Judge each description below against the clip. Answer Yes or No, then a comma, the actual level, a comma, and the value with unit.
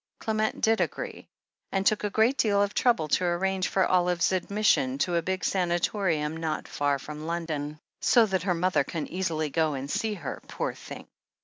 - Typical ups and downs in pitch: Yes, average, 4.2 semitones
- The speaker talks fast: No, average, 185 wpm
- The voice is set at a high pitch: No, medium, 180 Hz